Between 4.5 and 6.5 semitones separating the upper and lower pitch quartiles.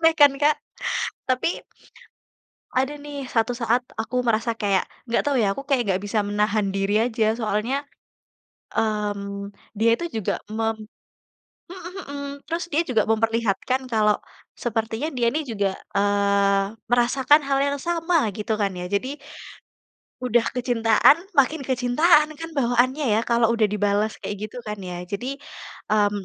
Yes: average, 4.8 semitones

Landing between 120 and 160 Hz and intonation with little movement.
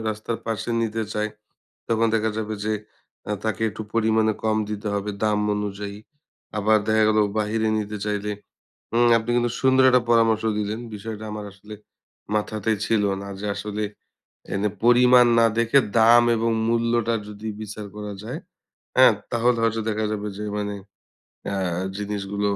No: low, 110 Hz; narrow, 1.6 semitones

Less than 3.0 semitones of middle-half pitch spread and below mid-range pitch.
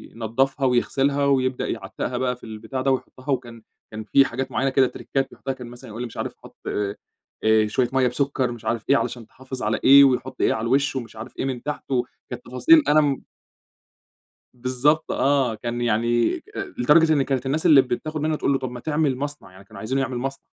Yes: narrow, 2.6 semitones; low, 130 Hz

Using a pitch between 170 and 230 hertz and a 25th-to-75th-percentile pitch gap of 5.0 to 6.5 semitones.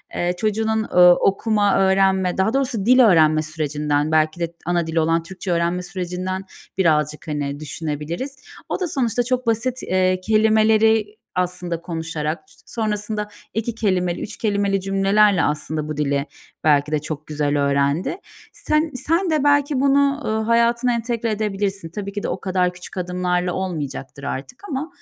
Yes: medium, 185 Hz; average, 5.3 semitones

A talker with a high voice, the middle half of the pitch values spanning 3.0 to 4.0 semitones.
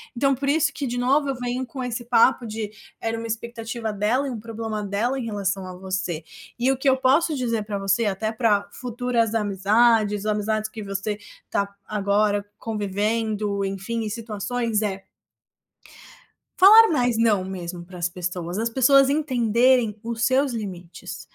Yes: high, 225 Hz; average, 3.4 semitones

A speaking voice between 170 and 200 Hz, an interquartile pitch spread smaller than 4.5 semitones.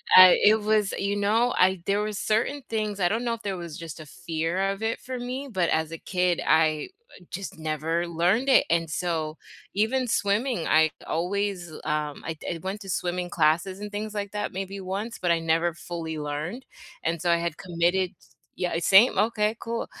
Yes: medium, 185 Hz; average, 4.1 semitones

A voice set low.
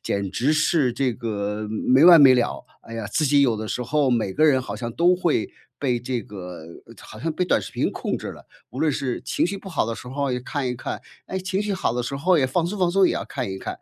Yes: low, 130 Hz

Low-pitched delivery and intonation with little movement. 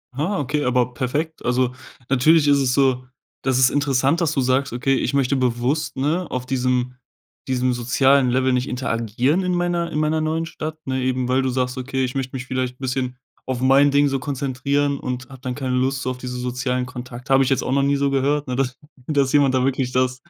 Yes: low, 130 Hz; narrow, 1.9 semitones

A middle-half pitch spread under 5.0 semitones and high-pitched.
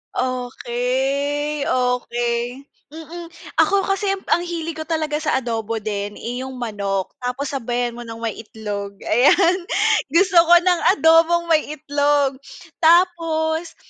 No: average, 5.3 semitones; very high, 275 Hz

